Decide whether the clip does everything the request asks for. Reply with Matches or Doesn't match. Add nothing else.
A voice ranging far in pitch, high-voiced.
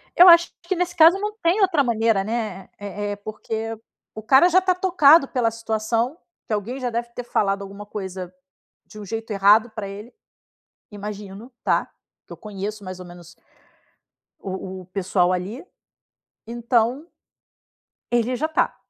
Doesn't match